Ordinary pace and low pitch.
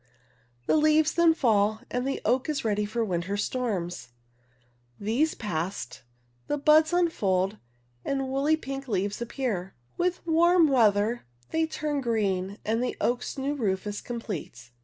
No: average, 160 wpm; high, 240 Hz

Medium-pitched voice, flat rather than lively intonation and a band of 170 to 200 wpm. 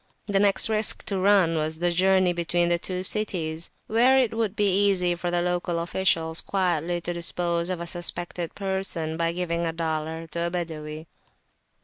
Yes: medium, 175 Hz; narrow, 2.3 semitones; average, 180 wpm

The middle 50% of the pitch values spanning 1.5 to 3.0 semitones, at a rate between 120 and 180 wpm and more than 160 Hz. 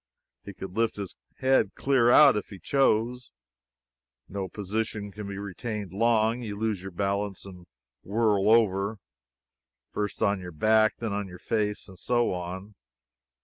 No: narrow, 2.5 semitones; average, 155 wpm; low, 105 Hz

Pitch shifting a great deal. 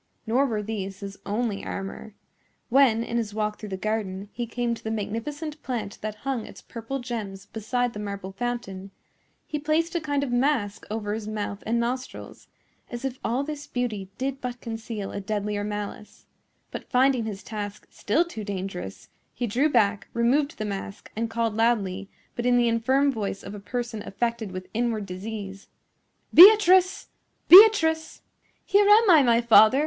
No: average, 3.9 semitones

